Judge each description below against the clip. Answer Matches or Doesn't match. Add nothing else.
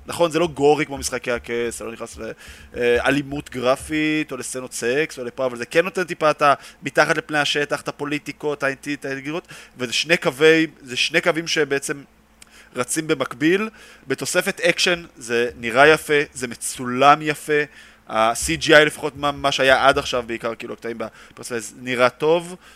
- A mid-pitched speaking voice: Matches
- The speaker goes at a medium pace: Doesn't match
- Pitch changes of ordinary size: Matches